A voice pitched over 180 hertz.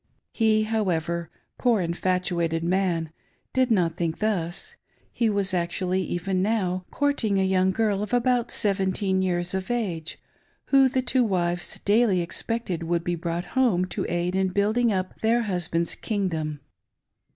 Yes: high, 190 Hz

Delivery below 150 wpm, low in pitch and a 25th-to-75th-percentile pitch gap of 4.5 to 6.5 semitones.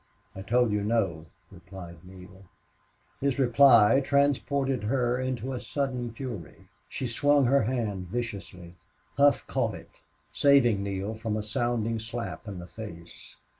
Yes: slow, 135 wpm; low, 115 Hz; average, 4.8 semitones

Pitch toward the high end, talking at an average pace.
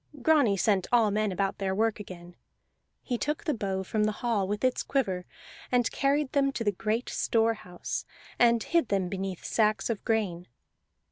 Yes: high, 215 Hz; average, 180 wpm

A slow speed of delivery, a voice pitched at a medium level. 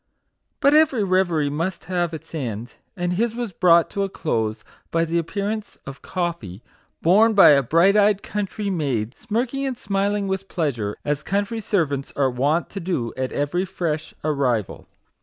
No: average, 165 wpm; medium, 175 Hz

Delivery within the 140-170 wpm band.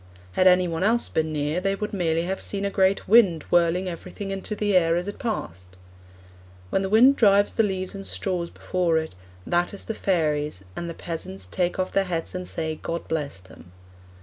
No: fast, 205 wpm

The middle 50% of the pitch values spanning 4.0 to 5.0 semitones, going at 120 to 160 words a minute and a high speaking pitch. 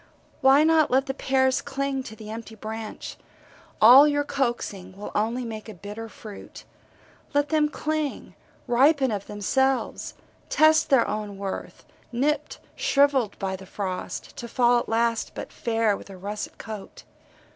Yes: average, 4.5 semitones; average, 150 wpm; high, 235 Hz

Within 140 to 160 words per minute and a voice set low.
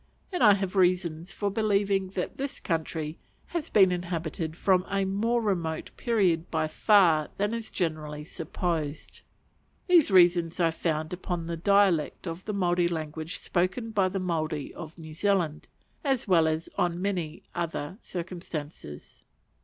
No: average, 145 wpm; medium, 175 Hz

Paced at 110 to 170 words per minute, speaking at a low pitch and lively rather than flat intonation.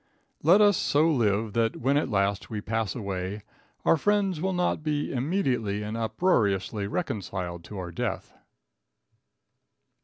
Yes: average, 140 wpm; low, 115 Hz; wide, 7.5 semitones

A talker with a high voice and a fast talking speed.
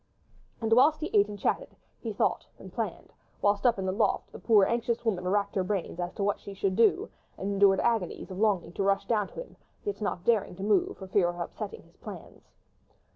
Yes: high, 200 Hz; fast, 225 wpm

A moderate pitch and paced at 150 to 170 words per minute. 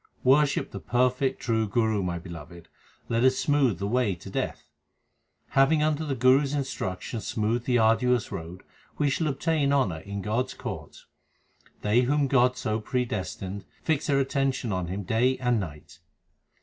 No: low, 125 Hz; average, 160 wpm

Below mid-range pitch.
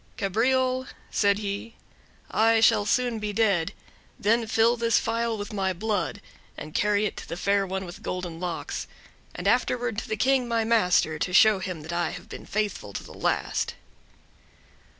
No: high, 210 Hz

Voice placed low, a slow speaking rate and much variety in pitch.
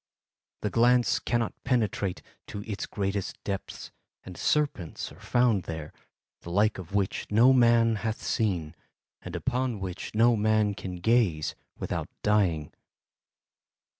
No: low, 105 Hz; slow, 130 wpm; average, 3.8 semitones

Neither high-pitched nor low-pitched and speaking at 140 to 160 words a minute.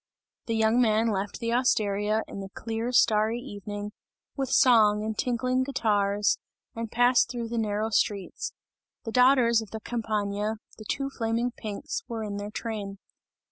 No: high, 220 Hz; average, 155 wpm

